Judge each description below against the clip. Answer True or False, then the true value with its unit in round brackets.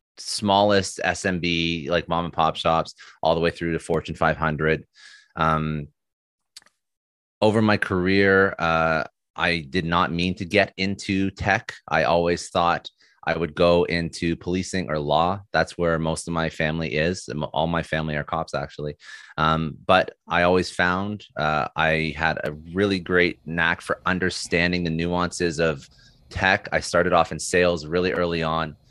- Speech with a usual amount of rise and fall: False (2.3 semitones)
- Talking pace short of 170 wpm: True (160 wpm)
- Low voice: True (85 Hz)